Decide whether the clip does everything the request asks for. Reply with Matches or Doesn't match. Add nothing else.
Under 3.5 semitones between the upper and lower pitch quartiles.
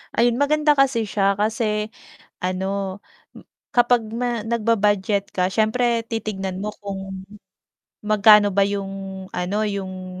Matches